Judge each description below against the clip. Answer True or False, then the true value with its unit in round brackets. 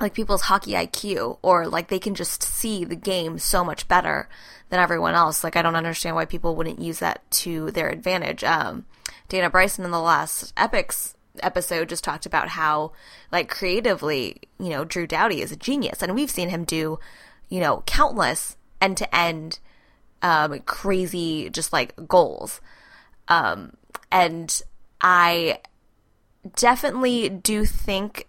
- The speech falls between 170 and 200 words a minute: False (155 wpm)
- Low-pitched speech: False (175 Hz)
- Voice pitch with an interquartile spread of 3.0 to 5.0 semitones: False (2.5 semitones)